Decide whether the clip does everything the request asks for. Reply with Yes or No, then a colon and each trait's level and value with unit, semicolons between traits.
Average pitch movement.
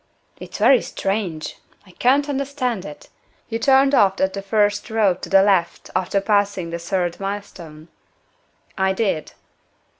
Yes: average, 3.3 semitones